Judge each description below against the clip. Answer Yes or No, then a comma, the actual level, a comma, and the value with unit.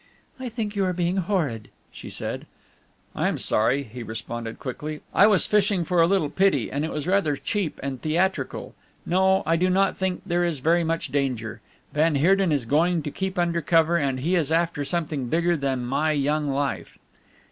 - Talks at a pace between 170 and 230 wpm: Yes, average, 190 wpm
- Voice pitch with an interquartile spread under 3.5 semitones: No, average, 4.7 semitones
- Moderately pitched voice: Yes, medium, 165 Hz